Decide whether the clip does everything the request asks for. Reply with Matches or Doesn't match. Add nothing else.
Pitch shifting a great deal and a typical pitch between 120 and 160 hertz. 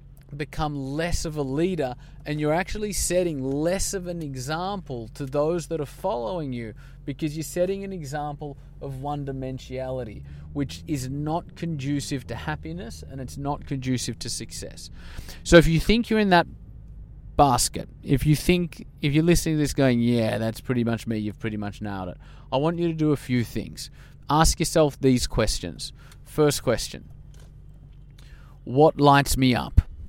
Doesn't match